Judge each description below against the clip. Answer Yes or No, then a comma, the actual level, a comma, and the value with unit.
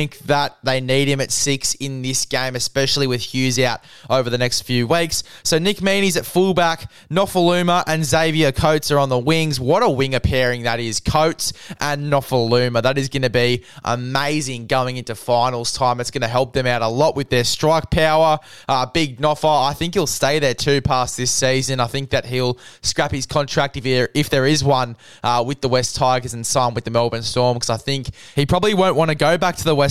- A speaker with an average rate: No, fast, 220 wpm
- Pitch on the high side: No, low, 135 Hz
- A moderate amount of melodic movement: Yes, average, 3.5 semitones